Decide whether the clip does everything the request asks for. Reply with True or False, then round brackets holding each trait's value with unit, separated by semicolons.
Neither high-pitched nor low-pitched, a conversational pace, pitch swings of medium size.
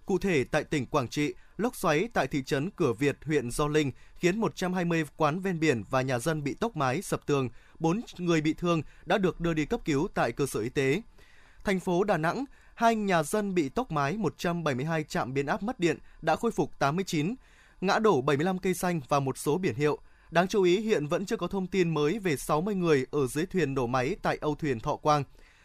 True (160 Hz; 225 wpm; 4.0 semitones)